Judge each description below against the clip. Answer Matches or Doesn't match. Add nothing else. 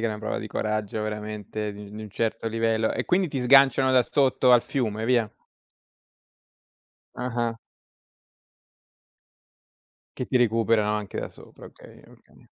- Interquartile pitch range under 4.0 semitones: Matches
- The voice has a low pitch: Matches